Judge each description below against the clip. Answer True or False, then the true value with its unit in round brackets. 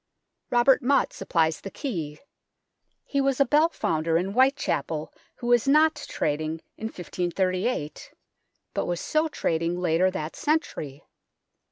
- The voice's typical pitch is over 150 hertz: True (190 Hz)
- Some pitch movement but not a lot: False (8.9 semitones)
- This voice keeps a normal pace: False (130 wpm)